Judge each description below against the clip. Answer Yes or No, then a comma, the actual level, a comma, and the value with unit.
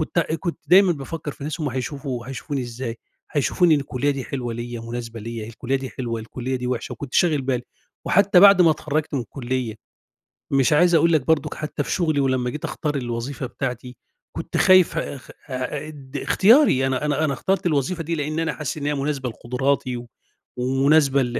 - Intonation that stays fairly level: No, average, 3.6 semitones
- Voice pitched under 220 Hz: Yes, medium, 140 Hz